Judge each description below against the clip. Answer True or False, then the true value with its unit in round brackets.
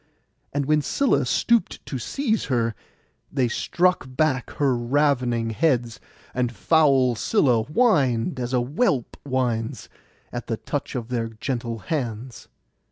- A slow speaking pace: True (130 wpm)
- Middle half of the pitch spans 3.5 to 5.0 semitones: True (3.9 semitones)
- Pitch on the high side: False (130 Hz)